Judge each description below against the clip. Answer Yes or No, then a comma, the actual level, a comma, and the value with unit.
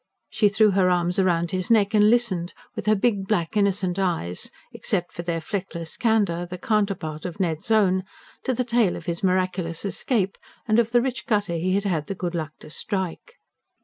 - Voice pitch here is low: No, high, 190 Hz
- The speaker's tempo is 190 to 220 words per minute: Yes, average, 195 wpm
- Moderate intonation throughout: Yes, average, 3.6 semitones